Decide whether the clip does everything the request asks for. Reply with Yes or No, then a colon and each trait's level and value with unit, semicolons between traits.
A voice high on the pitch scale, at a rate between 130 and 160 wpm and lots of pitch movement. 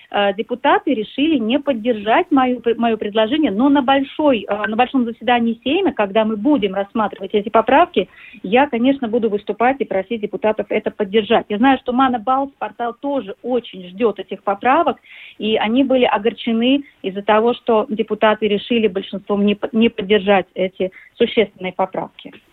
No: high, 230 Hz; average, 145 wpm; average, 3.5 semitones